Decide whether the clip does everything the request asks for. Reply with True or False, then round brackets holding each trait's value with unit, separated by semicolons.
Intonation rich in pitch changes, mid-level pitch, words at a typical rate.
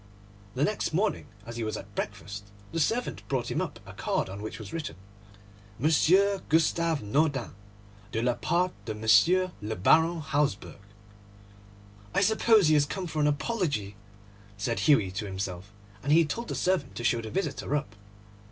True (7.6 semitones; 145 Hz; 170 wpm)